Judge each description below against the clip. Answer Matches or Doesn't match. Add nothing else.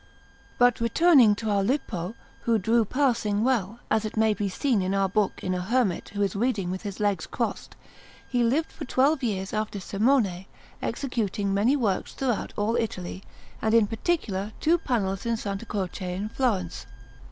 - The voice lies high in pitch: Matches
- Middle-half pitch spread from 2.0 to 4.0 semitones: Matches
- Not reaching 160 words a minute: Doesn't match